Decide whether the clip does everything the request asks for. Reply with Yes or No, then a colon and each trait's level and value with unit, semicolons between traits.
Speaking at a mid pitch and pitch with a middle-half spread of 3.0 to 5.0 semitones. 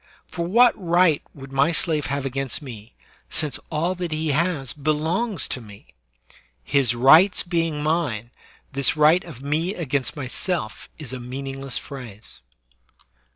Yes: medium, 150 Hz; average, 4.0 semitones